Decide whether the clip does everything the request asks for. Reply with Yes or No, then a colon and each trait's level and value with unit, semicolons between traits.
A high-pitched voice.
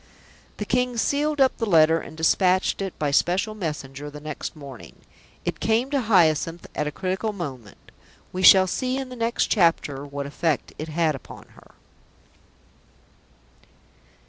No: medium, 175 Hz